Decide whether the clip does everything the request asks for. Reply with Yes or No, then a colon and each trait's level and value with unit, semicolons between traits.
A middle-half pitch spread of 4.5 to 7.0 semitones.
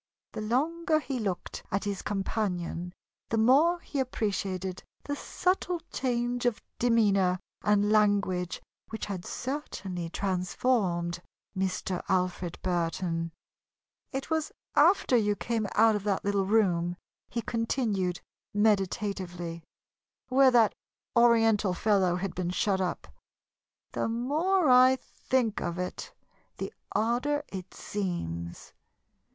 Yes: average, 4.9 semitones